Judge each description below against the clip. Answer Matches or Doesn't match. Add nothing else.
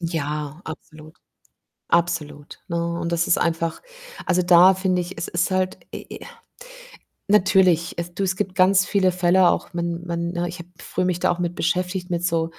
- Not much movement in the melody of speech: Matches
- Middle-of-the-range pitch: Matches